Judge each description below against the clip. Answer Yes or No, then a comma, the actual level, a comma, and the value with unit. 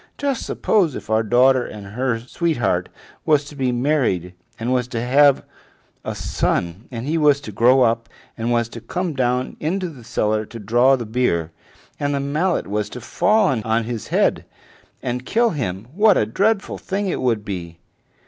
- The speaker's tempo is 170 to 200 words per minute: Yes, average, 180 wpm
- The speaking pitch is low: Yes, low, 125 Hz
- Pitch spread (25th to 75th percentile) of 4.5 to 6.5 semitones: Yes, average, 4.8 semitones